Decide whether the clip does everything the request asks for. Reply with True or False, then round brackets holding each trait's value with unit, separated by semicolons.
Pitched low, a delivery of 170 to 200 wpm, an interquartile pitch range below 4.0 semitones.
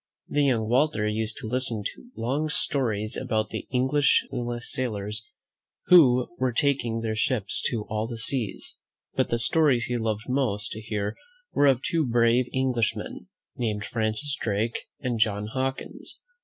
False (120 Hz; 155 wpm; 3.3 semitones)